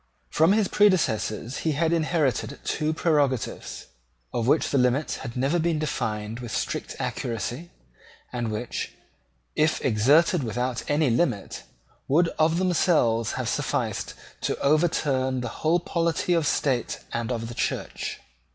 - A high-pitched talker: No, medium, 140 Hz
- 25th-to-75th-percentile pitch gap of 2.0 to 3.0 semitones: No, wide, 5.5 semitones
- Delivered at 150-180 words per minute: No, average, 140 wpm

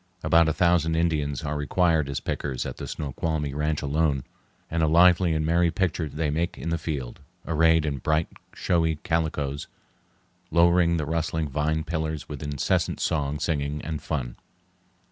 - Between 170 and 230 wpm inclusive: No, average, 160 wpm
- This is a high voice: No, very low, 80 Hz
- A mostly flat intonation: Yes, narrow, 2.1 semitones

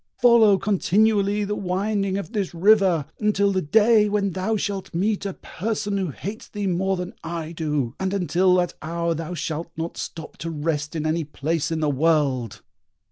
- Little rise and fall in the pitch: No, average, 3.9 semitones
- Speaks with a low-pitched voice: No, medium, 185 Hz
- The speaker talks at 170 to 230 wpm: Yes, average, 180 wpm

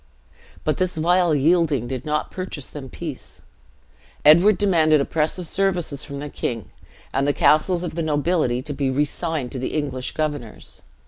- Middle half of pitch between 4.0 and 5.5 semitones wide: No, average, 3.6 semitones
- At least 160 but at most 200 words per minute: No, average, 150 wpm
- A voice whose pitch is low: No, medium, 150 Hz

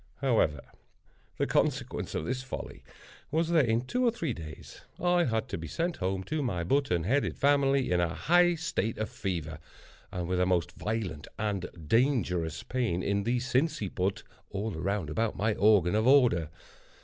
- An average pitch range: No, wide, 7.3 semitones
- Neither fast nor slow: Yes, average, 170 wpm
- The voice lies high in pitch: No, low, 110 Hz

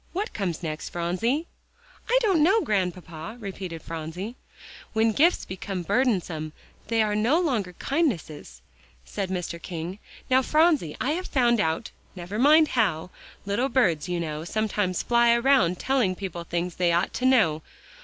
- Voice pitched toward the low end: No, high, 200 Hz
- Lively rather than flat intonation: Yes, wide, 6.8 semitones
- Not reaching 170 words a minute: Yes, average, 155 wpm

